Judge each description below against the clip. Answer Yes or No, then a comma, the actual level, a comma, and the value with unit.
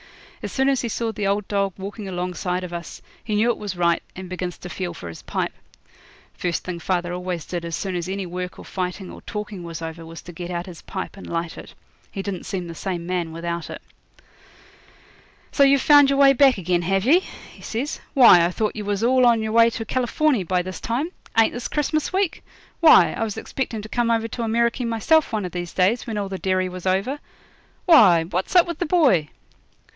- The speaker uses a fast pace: Yes, fast, 225 wpm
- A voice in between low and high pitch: No, high, 195 Hz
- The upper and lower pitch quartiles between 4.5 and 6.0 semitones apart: Yes, average, 4.8 semitones